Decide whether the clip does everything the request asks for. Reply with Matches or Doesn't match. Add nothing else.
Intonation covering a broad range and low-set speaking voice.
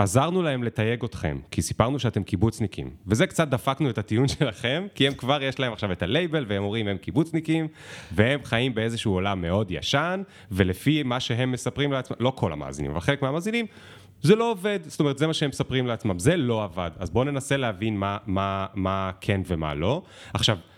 Matches